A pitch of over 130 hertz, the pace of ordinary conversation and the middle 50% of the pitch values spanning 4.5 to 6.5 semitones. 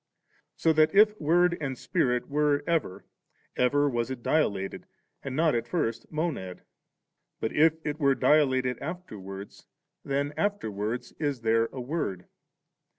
Yes: medium, 140 Hz; average, 145 wpm; average, 5.2 semitones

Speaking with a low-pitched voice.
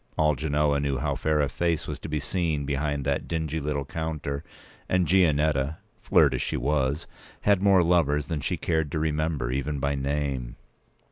Yes: very low, 75 Hz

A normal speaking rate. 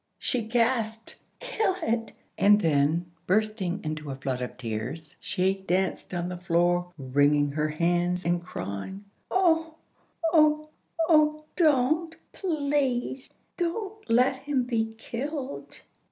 No: slow, 120 wpm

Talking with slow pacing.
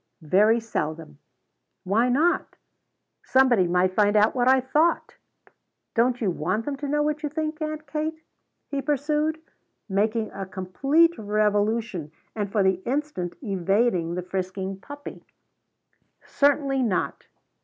Yes: slow, 130 wpm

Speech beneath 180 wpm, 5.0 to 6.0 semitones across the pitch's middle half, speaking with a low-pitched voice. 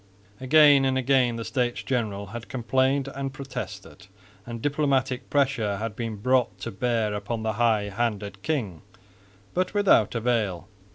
No: average, 140 wpm; average, 4.0 semitones; low, 120 Hz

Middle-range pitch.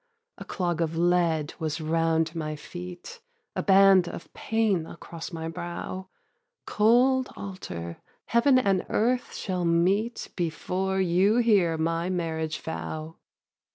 Yes: medium, 175 Hz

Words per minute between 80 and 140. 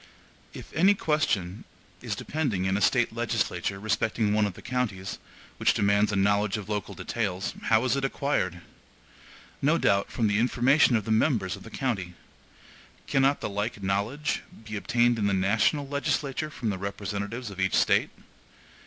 No: average, 165 wpm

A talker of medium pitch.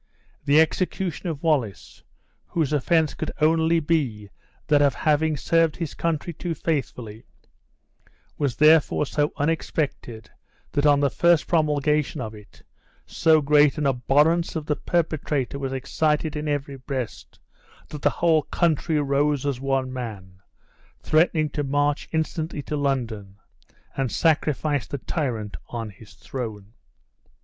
Yes: medium, 145 Hz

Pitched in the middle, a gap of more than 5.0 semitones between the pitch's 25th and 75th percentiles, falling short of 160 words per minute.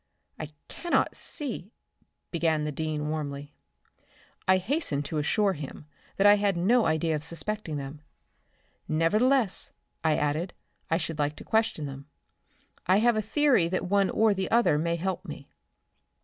Yes: medium, 170 Hz; wide, 5.6 semitones; average, 150 wpm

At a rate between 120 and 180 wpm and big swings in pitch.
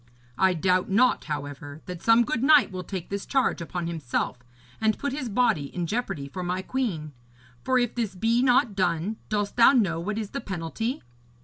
No: average, 190 wpm; wide, 5.9 semitones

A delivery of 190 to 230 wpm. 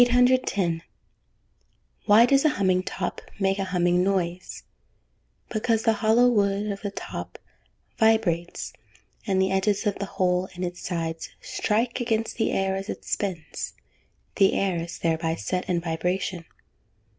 No: average, 145 wpm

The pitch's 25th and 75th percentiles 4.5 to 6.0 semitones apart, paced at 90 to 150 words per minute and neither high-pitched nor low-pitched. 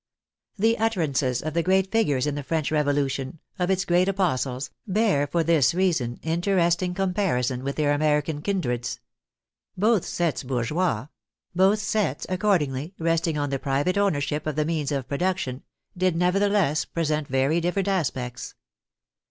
Yes: average, 4.9 semitones; average, 145 wpm; medium, 160 Hz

